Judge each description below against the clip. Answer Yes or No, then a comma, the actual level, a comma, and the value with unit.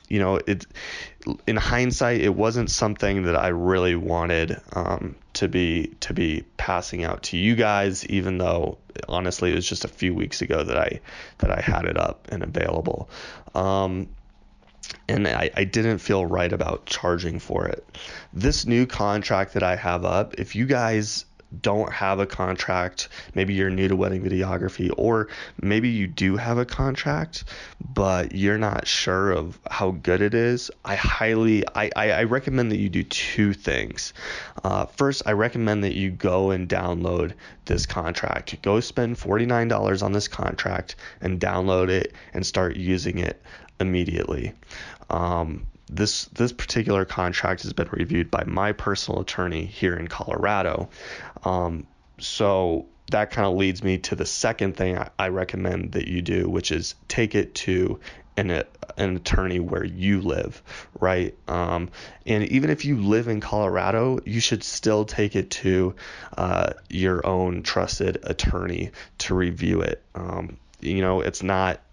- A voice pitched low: Yes, very low, 95 Hz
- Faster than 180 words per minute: No, average, 165 wpm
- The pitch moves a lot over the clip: No, average, 2.9 semitones